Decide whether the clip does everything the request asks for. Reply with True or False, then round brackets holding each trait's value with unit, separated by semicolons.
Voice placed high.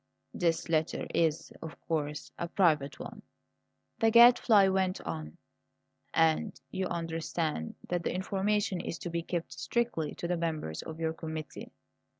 False (165 Hz)